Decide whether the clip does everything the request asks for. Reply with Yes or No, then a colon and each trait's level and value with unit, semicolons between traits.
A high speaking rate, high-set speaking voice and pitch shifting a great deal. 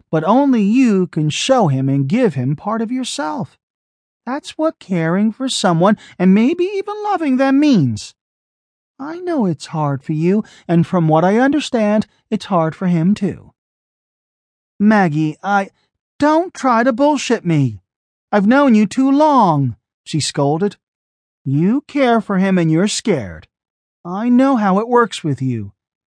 No: average, 155 wpm; high, 205 Hz; wide, 8.3 semitones